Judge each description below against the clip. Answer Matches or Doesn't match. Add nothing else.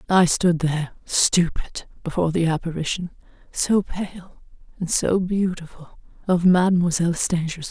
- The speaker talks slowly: Matches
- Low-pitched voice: Doesn't match